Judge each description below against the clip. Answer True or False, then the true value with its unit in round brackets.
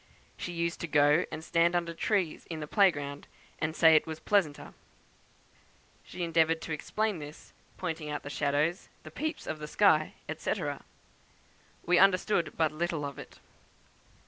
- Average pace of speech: True (160 wpm)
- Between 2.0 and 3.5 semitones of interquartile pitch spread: True (2.6 semitones)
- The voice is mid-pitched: True (165 Hz)